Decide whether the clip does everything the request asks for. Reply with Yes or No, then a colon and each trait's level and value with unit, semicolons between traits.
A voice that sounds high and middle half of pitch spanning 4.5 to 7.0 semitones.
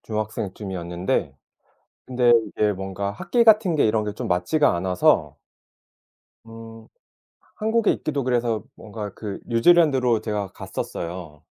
No: low, 110 Hz; average, 4.8 semitones